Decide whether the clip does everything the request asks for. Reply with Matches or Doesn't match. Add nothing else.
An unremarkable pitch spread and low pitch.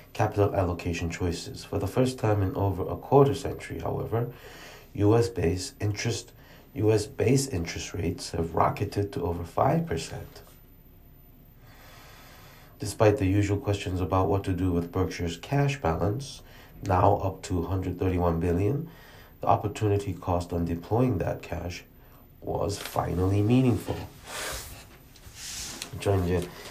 Matches